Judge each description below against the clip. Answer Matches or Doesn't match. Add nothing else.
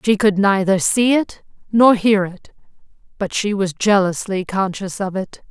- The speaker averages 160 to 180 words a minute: Matches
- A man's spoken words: Doesn't match